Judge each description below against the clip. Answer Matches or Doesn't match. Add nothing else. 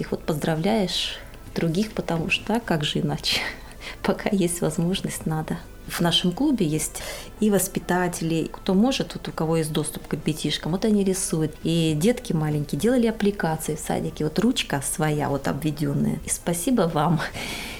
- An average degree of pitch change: Matches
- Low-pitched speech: Doesn't match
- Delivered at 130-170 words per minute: Matches